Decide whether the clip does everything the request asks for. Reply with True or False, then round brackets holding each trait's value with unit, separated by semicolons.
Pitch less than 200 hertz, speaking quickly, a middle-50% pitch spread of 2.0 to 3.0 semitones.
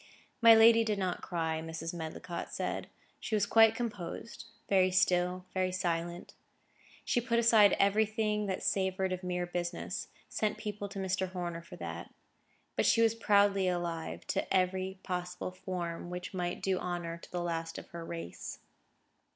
False (185 Hz; 160 wpm; 2.7 semitones)